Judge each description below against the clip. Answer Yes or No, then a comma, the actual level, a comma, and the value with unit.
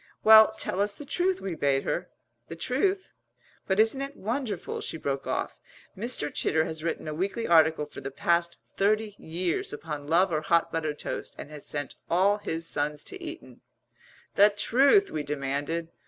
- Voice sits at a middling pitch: Yes, medium, 170 Hz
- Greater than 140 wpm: Yes, average, 180 wpm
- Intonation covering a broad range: Yes, wide, 6.0 semitones